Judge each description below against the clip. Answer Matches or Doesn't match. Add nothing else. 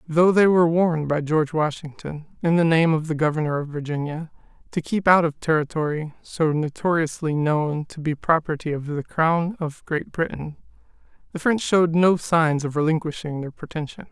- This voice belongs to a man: Matches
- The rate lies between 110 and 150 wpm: Doesn't match